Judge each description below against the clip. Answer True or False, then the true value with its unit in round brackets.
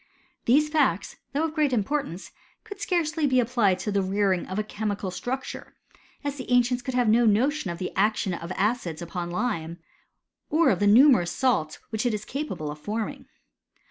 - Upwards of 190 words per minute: False (175 wpm)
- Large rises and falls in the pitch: True (5.8 semitones)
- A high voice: True (220 Hz)